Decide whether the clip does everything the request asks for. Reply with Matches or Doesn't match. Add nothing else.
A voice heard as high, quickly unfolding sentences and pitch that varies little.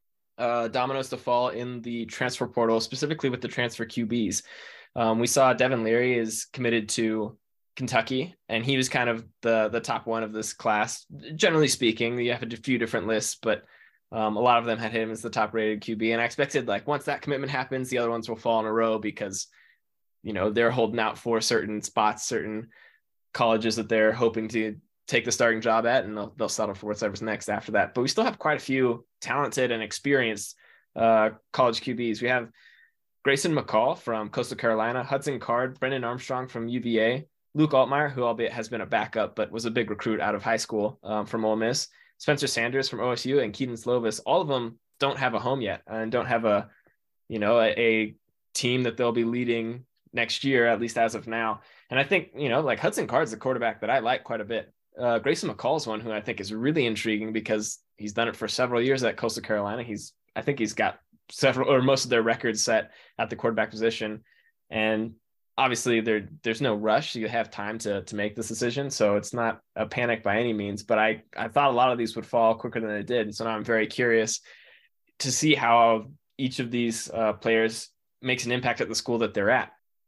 Doesn't match